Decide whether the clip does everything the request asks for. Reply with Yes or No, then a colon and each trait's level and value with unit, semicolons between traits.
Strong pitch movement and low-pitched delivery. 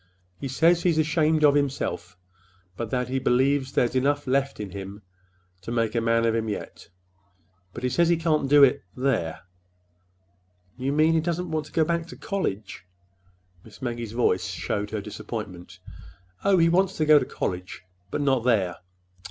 Yes: wide, 6.4 semitones; low, 130 Hz